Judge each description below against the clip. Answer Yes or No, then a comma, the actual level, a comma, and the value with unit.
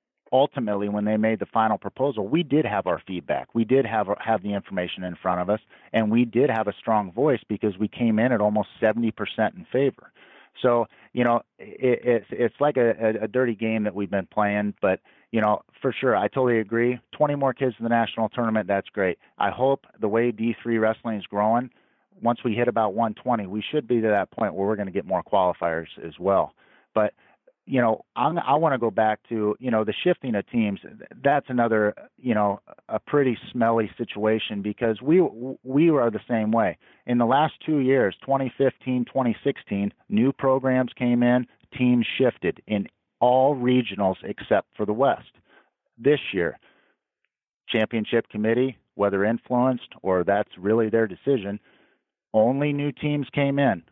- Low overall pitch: Yes, low, 115 Hz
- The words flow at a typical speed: Yes, average, 185 wpm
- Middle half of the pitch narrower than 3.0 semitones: No, average, 3.3 semitones